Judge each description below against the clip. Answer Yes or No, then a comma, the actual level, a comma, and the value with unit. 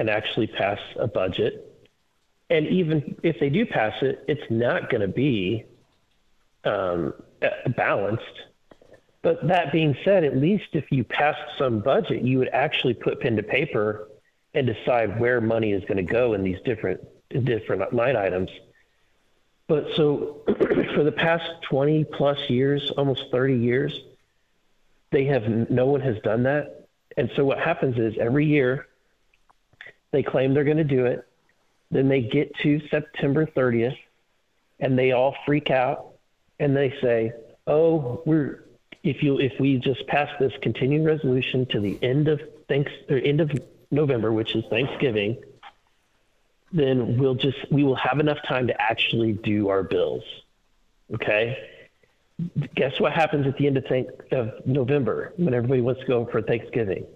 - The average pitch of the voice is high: No, medium, 140 Hz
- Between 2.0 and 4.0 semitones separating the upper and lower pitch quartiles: Yes, average, 3.2 semitones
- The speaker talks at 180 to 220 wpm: No, average, 155 wpm